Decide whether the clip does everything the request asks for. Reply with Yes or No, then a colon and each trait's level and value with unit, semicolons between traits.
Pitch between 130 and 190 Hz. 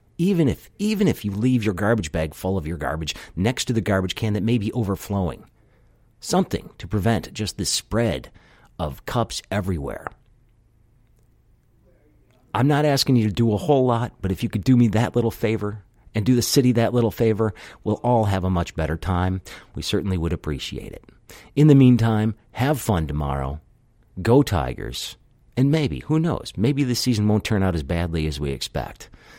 No: low, 110 Hz